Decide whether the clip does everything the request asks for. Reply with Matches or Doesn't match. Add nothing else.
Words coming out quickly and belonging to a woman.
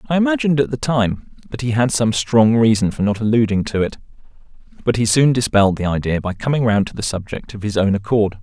Doesn't match